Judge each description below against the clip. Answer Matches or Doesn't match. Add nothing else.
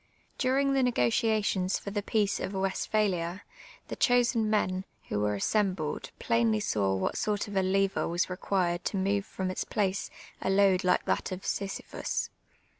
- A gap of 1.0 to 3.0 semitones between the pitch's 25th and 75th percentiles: Matches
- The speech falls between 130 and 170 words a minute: Matches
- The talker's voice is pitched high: Matches